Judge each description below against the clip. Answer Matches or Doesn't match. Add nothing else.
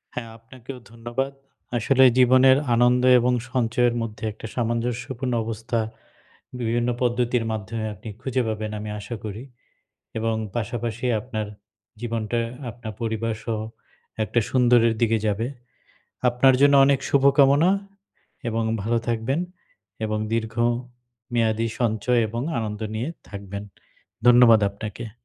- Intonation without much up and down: Matches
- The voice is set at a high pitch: Doesn't match